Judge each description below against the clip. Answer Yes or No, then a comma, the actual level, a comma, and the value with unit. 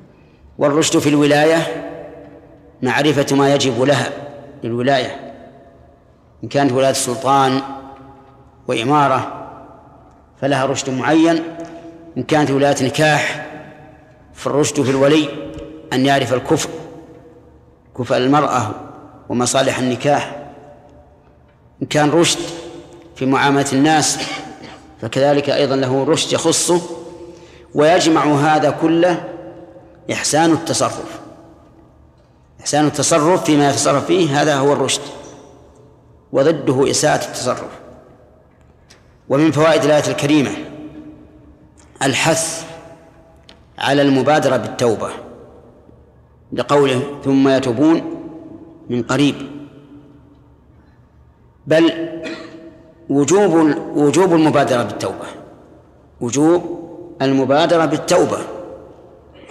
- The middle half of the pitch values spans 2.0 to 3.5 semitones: Yes, average, 3.0 semitones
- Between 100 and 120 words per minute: No, average, 80 wpm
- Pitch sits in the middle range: Yes, medium, 145 Hz